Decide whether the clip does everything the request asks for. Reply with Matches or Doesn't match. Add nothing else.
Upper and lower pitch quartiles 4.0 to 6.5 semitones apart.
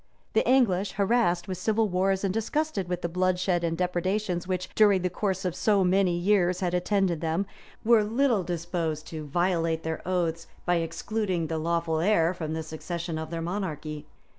Doesn't match